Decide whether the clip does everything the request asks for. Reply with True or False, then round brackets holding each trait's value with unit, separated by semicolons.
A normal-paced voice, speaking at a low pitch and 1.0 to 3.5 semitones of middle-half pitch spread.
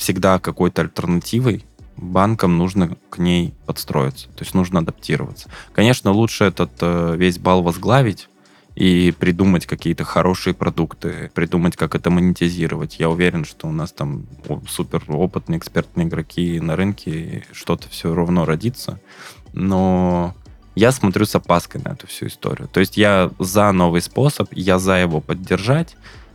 True (145 wpm; 90 Hz; 2.4 semitones)